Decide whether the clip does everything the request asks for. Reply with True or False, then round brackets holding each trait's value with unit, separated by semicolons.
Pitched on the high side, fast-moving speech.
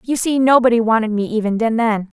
False (230 Hz; 190 wpm)